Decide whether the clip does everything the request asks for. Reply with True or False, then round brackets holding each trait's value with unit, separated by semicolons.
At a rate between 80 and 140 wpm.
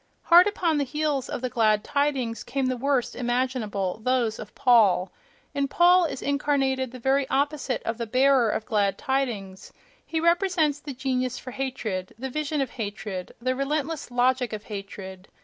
False (165 wpm)